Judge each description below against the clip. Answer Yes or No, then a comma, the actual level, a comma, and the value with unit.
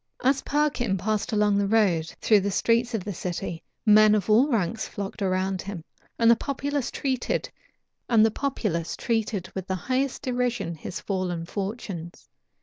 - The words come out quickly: No, average, 145 wpm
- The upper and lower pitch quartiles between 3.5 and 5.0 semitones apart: Yes, average, 4.2 semitones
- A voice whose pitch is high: Yes, high, 210 Hz